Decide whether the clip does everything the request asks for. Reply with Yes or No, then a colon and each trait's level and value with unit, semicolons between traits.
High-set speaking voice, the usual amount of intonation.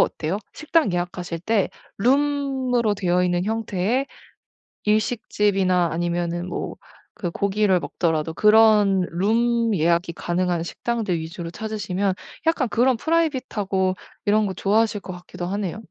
Yes: high, 200 Hz; average, 4.2 semitones